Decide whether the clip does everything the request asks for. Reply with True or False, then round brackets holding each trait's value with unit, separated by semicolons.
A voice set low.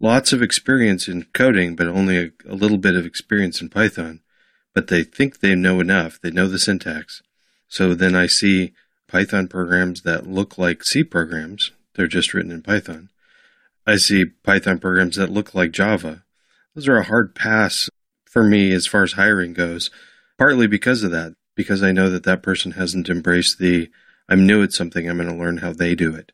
True (90 Hz)